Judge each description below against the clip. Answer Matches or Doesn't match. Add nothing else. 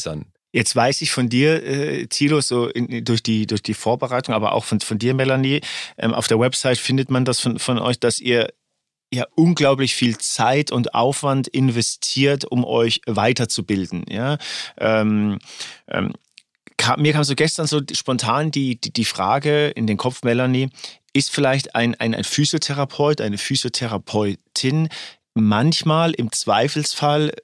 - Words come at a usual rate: Matches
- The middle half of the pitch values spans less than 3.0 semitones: Doesn't match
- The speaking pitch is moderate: Doesn't match